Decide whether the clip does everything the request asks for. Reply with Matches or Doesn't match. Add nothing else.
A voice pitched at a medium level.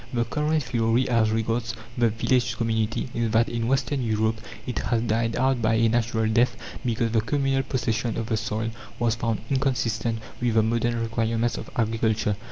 Doesn't match